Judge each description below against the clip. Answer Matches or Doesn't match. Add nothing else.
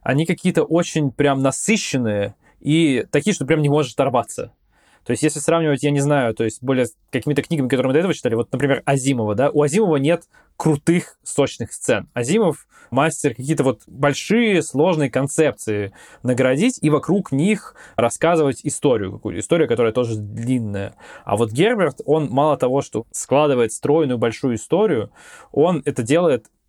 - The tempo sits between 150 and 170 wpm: Matches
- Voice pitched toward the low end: Doesn't match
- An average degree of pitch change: Matches